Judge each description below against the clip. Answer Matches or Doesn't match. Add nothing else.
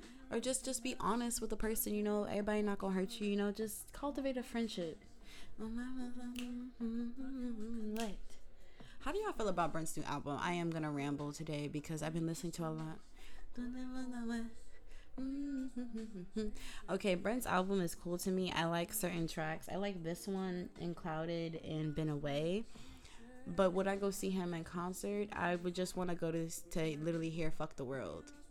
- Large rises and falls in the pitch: Matches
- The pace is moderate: Matches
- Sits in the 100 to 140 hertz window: Doesn't match